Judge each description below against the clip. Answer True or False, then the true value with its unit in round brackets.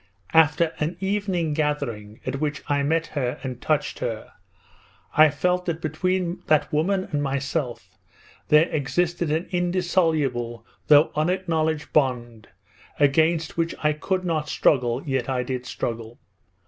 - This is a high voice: False (155 Hz)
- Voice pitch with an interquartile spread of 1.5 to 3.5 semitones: False (4.1 semitones)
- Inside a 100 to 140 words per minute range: True (135 wpm)